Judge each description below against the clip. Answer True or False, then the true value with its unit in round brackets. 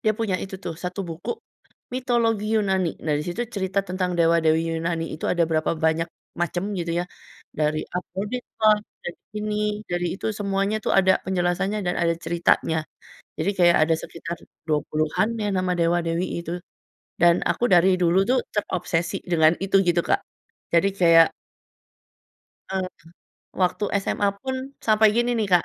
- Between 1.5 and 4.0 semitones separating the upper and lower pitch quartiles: True (3.1 semitones)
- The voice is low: False (180 Hz)